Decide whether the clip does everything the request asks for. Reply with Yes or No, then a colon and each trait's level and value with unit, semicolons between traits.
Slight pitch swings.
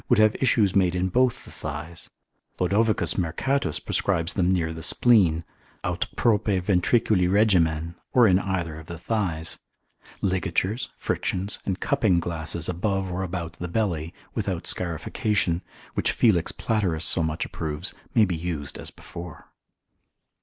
No: average, 3.8 semitones